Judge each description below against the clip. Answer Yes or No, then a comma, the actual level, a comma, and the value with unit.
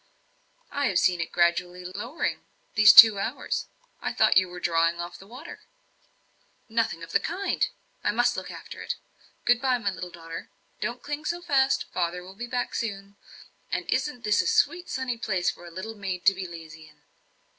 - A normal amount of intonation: No, wide, 5.8 semitones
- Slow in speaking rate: No, average, 190 wpm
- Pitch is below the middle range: No, high, 200 Hz